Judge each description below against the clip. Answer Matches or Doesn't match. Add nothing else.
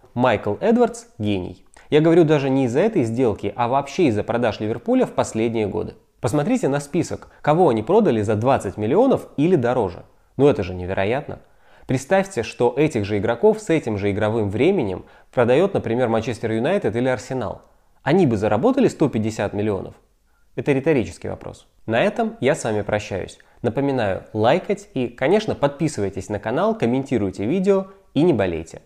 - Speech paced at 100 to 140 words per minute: Doesn't match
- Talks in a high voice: Doesn't match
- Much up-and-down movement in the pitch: Matches